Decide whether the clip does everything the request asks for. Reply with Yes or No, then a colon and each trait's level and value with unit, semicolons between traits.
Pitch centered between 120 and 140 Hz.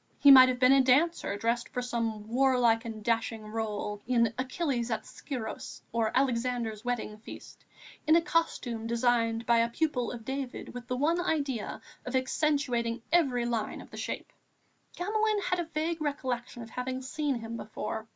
No: high, 245 Hz